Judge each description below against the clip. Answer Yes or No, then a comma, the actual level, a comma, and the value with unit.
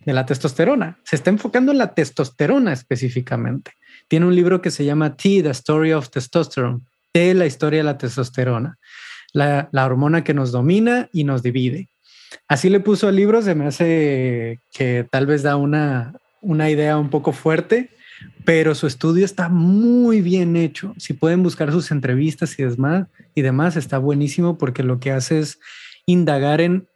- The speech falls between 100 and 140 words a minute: No, average, 170 wpm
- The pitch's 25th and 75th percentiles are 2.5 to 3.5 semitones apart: No, average, 4.5 semitones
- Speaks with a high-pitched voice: No, medium, 155 Hz